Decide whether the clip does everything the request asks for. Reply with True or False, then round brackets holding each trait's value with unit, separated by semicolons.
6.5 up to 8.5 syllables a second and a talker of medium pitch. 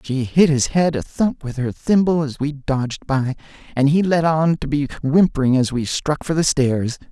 False (4.7 syllables/s; 145 Hz)